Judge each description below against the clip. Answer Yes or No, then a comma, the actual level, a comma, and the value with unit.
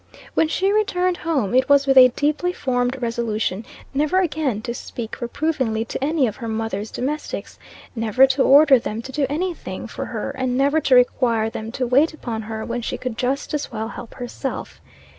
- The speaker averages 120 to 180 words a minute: No, average, 195 wpm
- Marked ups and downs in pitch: No, average, 4.3 semitones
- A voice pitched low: No, very high, 255 Hz